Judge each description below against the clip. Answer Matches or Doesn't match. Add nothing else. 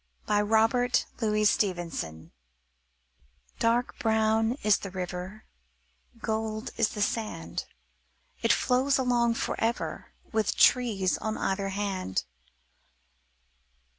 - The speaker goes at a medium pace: Doesn't match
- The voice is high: Matches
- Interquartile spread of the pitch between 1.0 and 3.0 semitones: Matches